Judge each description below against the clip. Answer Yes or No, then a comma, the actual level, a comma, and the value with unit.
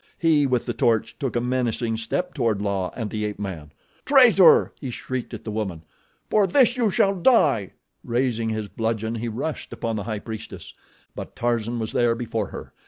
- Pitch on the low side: Yes, low, 115 Hz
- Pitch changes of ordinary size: Yes, average, 3.9 semitones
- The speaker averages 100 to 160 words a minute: No, average, 190 wpm